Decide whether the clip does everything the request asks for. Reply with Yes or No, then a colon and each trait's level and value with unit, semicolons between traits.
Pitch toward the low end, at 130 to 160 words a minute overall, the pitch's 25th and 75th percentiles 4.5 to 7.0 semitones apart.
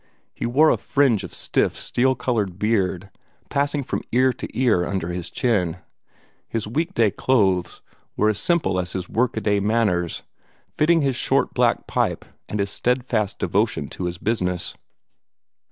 Yes: low, 110 Hz; average, 155 wpm; wide, 5.5 semitones